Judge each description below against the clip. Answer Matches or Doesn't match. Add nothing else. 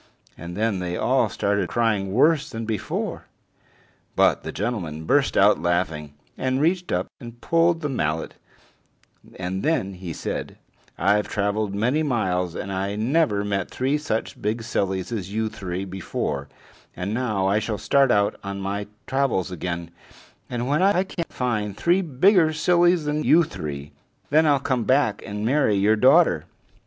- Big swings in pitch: Matches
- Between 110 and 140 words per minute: Doesn't match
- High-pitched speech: Doesn't match